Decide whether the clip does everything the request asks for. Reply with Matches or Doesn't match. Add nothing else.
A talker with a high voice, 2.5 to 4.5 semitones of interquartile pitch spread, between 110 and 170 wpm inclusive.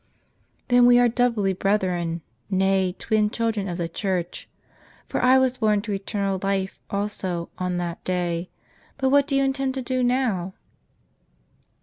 Doesn't match